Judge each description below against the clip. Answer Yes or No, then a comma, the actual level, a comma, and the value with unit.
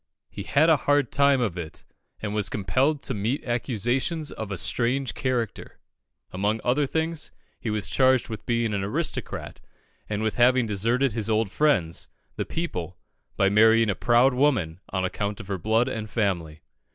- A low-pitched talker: Yes, low, 115 Hz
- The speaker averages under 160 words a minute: No, average, 170 wpm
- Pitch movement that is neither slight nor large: Yes, average, 4.4 semitones